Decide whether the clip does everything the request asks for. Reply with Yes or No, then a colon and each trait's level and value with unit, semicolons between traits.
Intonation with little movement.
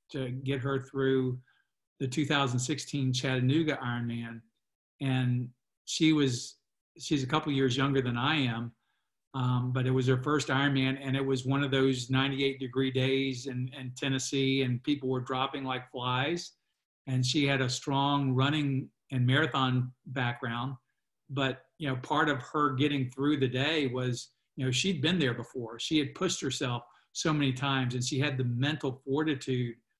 Yes: narrow, 1.8 semitones